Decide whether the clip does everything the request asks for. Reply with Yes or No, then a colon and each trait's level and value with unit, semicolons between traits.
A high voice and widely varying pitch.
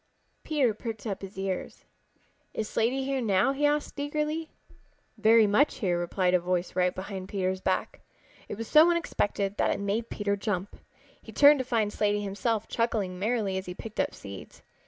No: high, 210 Hz; average, 4.5 semitones